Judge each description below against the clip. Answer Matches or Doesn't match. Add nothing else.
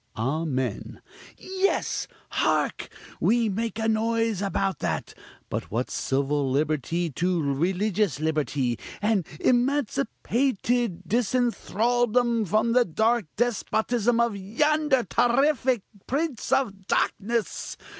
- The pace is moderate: Doesn't match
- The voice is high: Matches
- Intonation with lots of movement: Matches